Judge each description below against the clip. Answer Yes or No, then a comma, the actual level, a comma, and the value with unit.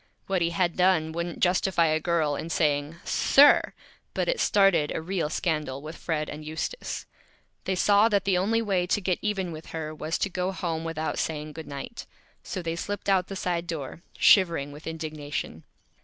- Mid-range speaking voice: Yes, medium, 170 Hz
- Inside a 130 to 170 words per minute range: No, average, 185 wpm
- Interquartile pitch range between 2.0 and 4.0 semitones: Yes, average, 3.3 semitones